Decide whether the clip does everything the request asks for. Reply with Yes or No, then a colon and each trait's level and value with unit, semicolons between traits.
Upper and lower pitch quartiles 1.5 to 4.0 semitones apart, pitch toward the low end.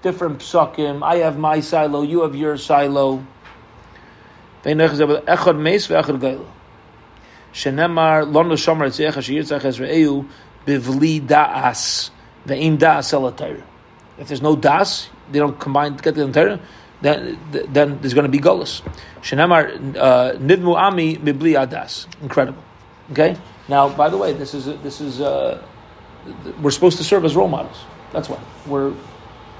No: narrow, 2.4 semitones; medium, 145 Hz